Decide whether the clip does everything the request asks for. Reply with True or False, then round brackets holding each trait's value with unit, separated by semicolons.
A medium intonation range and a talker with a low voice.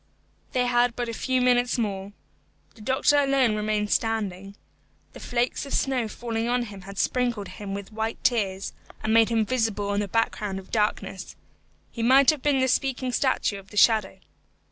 False (3.4 semitones; 225 Hz)